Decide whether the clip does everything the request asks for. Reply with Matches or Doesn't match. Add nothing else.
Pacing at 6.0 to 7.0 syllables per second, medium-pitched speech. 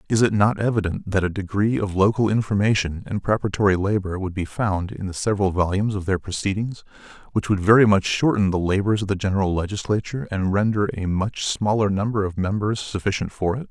Doesn't match